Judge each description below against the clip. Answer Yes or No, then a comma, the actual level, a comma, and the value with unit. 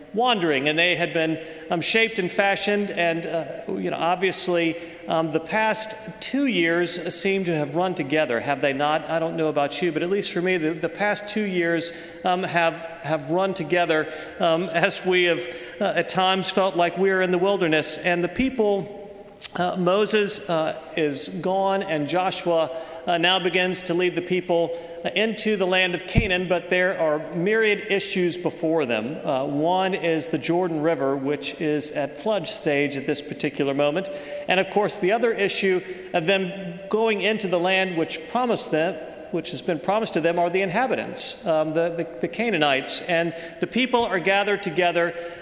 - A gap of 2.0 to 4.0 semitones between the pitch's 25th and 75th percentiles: Yes, average, 3.0 semitones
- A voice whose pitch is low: No, medium, 175 Hz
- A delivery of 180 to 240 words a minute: Yes, average, 185 wpm